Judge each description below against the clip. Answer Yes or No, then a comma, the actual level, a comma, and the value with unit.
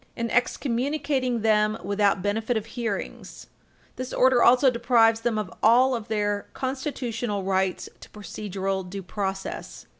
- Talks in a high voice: Yes, high, 220 Hz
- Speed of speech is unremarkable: No, slow, 125 wpm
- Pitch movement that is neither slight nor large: Yes, average, 3.4 semitones